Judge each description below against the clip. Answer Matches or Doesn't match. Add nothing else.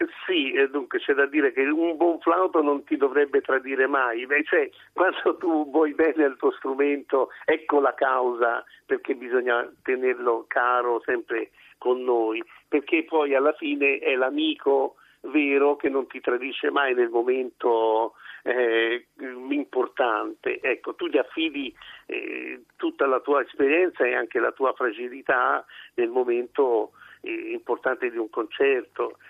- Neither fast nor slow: Matches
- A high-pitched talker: Matches